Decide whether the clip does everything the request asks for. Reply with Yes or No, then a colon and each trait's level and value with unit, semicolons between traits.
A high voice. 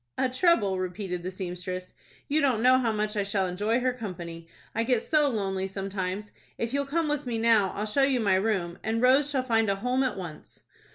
Yes: high, 215 Hz